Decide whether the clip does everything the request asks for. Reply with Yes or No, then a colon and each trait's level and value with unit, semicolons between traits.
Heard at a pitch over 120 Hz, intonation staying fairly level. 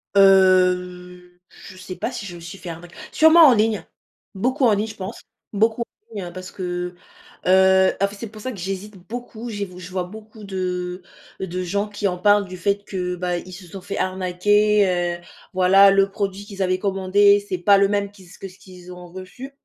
Yes: high, 190 Hz; narrow, 2.2 semitones